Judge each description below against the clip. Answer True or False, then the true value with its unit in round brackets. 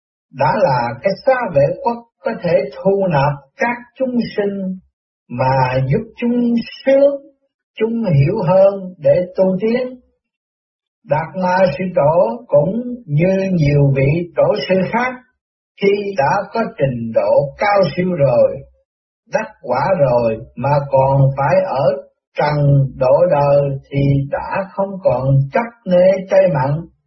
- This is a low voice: False (185 Hz)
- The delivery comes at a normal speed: False (135 wpm)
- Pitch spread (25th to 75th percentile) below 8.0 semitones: False (8.7 semitones)